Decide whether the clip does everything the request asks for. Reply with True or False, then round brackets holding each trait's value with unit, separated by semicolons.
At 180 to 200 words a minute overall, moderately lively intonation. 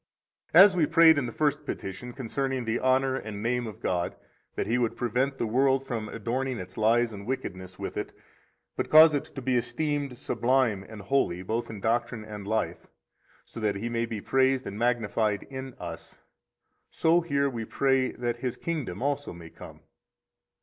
True (185 wpm; 3.7 semitones)